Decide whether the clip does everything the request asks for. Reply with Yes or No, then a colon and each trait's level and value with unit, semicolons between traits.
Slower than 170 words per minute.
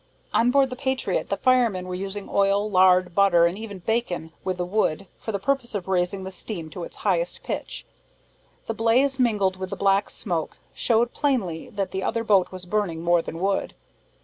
No: average, 195 wpm